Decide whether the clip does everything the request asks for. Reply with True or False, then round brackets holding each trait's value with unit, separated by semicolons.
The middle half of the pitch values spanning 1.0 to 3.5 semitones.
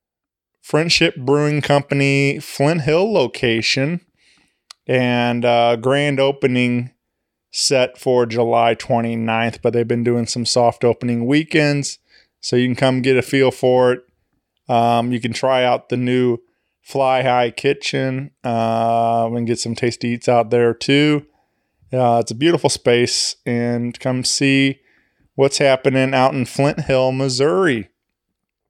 True (2.6 semitones)